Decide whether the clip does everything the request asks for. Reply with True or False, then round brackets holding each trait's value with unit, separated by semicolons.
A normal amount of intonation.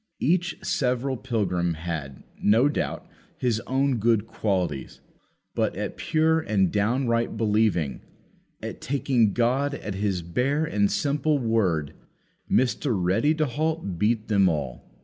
False (6.2 semitones)